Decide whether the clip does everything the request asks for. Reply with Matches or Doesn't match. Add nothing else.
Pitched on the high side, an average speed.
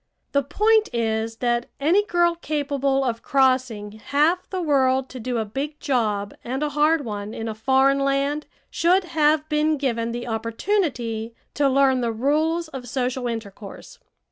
Matches